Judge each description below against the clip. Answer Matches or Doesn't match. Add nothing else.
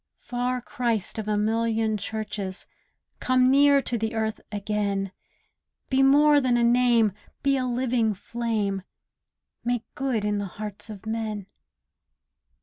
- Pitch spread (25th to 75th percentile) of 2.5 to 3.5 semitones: Matches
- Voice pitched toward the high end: Matches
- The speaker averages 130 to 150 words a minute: Matches